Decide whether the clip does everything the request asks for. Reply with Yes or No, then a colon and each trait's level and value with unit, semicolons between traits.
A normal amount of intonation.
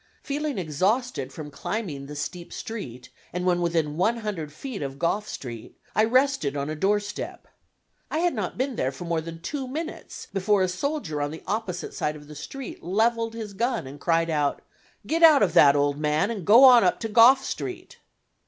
No: wide, 7.5 semitones